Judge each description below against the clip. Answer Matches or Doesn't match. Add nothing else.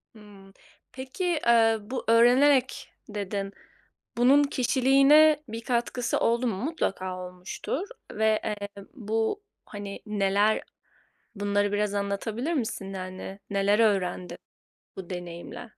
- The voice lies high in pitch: Matches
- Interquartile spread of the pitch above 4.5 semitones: Doesn't match